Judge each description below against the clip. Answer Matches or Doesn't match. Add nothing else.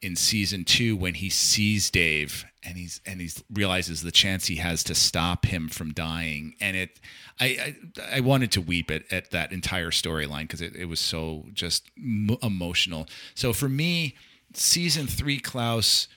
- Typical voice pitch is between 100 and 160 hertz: Doesn't match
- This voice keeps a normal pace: Matches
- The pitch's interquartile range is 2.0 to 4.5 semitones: Doesn't match